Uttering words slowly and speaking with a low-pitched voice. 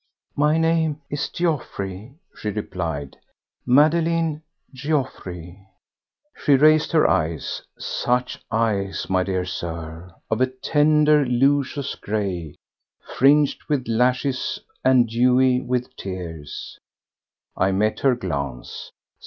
Yes: slow, 95 wpm; low, 125 Hz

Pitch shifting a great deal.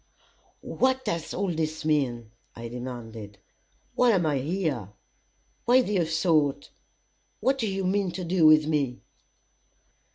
Yes: wide, 6.7 semitones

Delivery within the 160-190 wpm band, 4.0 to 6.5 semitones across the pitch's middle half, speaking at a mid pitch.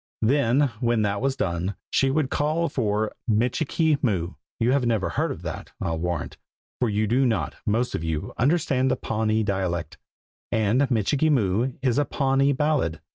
No: average, 165 wpm; average, 4.9 semitones; low, 120 Hz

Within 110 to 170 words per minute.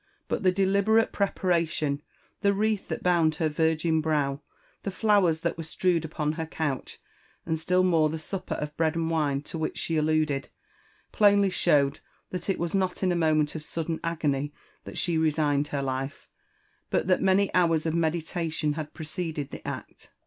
No: average, 180 wpm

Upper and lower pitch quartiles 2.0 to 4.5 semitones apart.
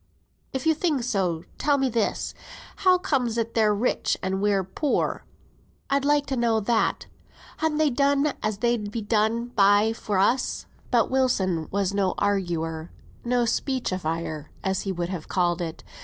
No: average, 5.3 semitones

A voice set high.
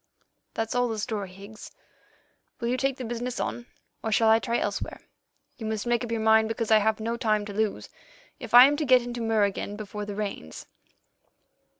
Yes: high, 225 Hz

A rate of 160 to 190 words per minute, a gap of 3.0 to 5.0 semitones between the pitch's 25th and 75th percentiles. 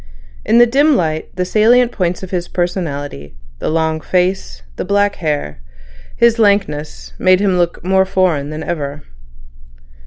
No: average, 150 wpm; average, 4.5 semitones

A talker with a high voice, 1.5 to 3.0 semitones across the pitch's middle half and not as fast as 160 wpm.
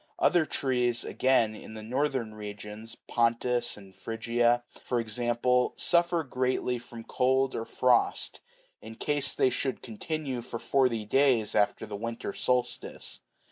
No: low, 120 Hz; narrow, 2.5 semitones; slow, 135 wpm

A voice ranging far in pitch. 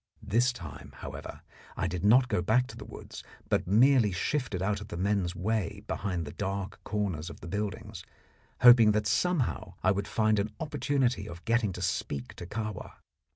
No: average, 3.8 semitones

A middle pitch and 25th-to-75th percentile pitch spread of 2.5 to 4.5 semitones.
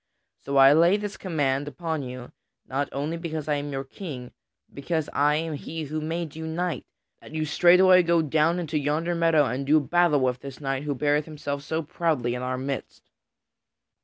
Yes: medium, 150 Hz; average, 3.0 semitones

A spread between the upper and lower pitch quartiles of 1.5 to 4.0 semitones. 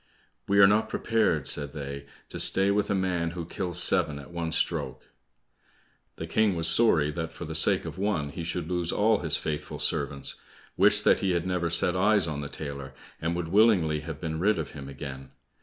No: average, 4.4 semitones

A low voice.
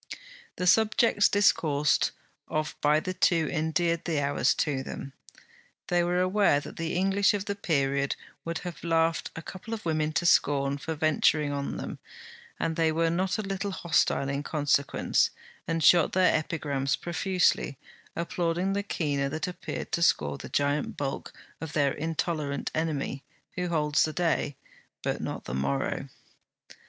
No: medium, 160 Hz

